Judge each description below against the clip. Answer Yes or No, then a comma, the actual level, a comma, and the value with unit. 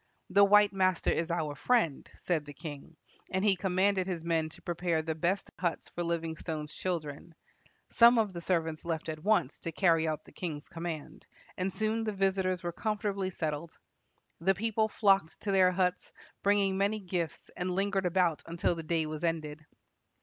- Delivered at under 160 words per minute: No, average, 175 wpm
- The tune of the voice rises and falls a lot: No, average, 3.2 semitones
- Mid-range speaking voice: Yes, medium, 175 Hz